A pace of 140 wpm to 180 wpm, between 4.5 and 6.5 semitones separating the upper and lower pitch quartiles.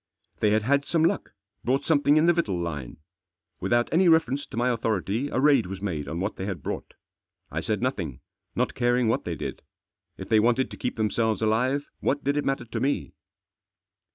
No: fast, 205 wpm; average, 5.2 semitones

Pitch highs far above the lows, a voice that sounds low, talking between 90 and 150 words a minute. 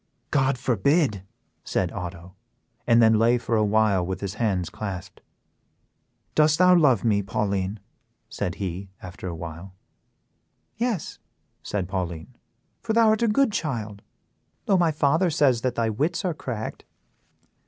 Yes: wide, 7.8 semitones; low, 110 Hz; average, 145 wpm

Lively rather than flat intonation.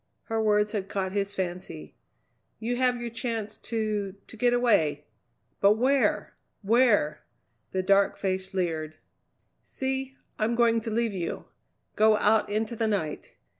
No: average, 3.4 semitones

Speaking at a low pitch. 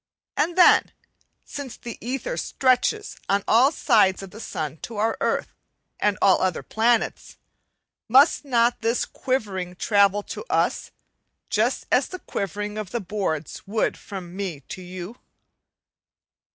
No: high, 210 Hz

